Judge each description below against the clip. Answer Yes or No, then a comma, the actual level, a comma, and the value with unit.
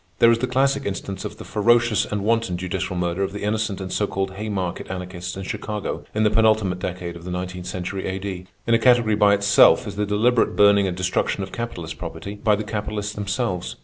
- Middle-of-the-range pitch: No, low, 100 Hz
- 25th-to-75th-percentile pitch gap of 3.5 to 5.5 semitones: No, average, 2.8 semitones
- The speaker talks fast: Yes, fast, 210 wpm